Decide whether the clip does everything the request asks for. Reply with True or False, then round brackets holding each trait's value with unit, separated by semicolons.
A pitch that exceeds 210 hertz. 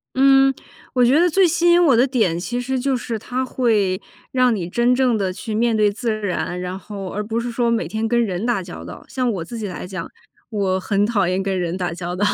True (220 Hz)